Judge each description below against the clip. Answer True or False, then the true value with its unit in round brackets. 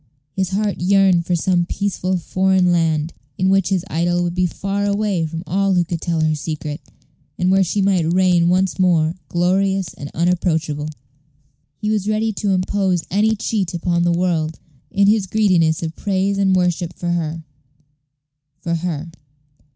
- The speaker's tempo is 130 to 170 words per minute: True (165 wpm)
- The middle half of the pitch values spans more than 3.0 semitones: False (2.5 semitones)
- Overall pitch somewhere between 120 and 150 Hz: False (180 Hz)